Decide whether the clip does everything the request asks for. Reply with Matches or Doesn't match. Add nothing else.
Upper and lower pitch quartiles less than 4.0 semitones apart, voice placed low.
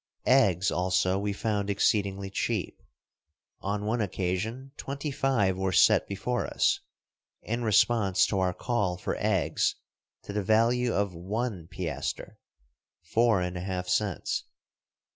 Matches